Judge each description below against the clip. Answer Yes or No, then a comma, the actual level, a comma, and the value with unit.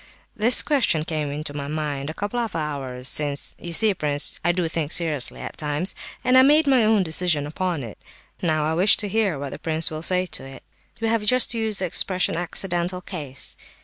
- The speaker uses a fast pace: Yes, fast, 210 wpm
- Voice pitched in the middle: Yes, medium, 170 Hz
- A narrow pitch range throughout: No, wide, 5.4 semitones